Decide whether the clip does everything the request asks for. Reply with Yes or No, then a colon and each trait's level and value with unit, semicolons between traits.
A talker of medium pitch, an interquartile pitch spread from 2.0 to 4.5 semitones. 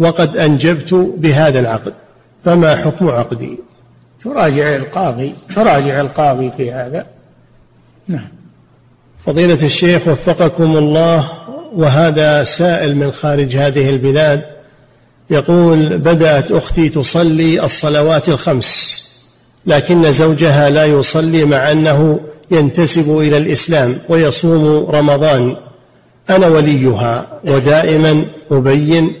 Yes: medium, 150 Hz; narrow, 2.5 semitones